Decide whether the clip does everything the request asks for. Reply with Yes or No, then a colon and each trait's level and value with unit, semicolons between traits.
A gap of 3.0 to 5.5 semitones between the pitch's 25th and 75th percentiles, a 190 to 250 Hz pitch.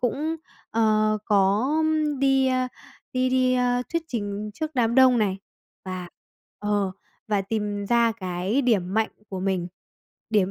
Yes: average, 4.2 semitones; high, 215 Hz